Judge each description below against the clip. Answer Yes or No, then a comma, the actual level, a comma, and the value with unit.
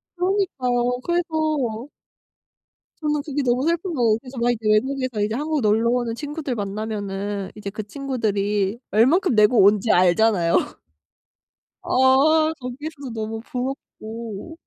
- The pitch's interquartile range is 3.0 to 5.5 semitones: Yes, average, 5.1 semitones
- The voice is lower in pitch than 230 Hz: No, high, 245 Hz